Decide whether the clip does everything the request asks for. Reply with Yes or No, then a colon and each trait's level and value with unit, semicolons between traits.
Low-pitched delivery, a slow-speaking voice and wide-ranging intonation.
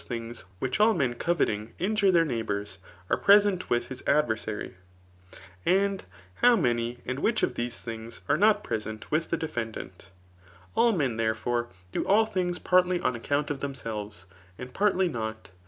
No: low, 130 Hz; average, 155 wpm; wide, 8.1 semitones